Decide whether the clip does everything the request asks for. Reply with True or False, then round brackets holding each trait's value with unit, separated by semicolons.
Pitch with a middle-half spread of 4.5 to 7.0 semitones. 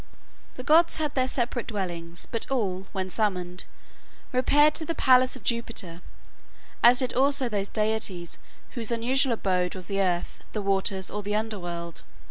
True (5.4 semitones)